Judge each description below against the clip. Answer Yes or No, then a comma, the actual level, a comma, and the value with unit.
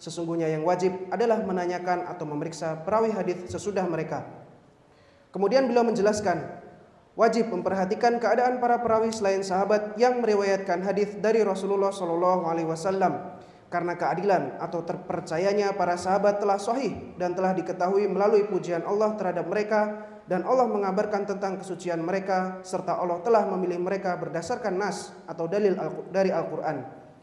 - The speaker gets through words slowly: No, average, 135 wpm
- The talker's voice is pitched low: No, medium, 185 Hz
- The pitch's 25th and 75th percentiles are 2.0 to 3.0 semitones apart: Yes, average, 2.7 semitones